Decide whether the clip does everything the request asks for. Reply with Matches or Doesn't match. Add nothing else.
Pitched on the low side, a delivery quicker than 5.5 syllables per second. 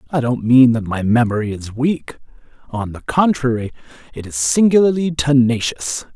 Doesn't match